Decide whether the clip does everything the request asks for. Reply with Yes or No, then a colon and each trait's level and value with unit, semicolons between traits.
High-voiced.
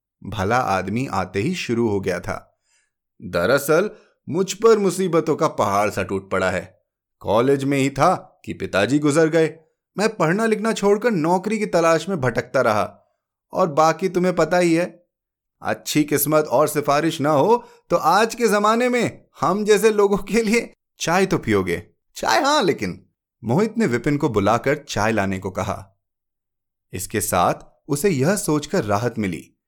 No: medium, 150 Hz